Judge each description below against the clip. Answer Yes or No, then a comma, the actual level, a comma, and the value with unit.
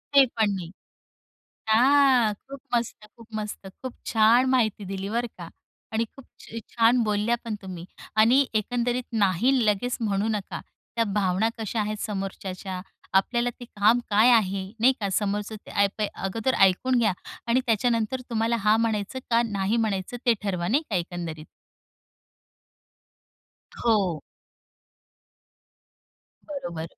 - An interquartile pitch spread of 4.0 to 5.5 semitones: No, average, 3.4 semitones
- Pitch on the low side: No, high, 215 Hz